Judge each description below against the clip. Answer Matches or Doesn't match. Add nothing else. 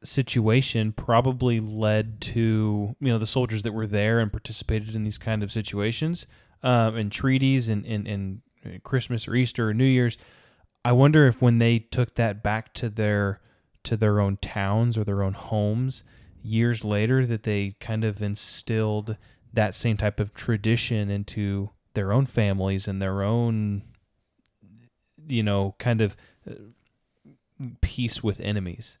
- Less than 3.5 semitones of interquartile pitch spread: Matches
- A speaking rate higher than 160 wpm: Doesn't match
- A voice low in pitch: Matches